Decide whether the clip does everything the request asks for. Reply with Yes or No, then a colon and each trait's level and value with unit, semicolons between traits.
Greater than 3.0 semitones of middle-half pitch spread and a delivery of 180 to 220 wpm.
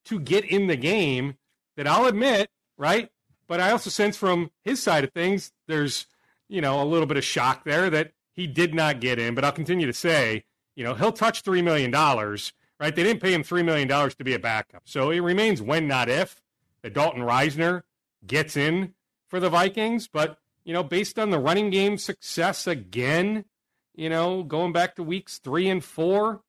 Yes: average, 4.7 semitones; average, 200 wpm